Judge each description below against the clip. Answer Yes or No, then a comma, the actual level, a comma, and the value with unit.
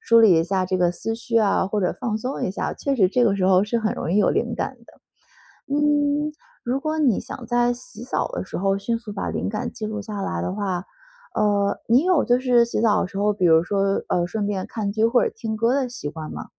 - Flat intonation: No, average, 3.7 semitones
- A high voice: Yes, high, 215 Hz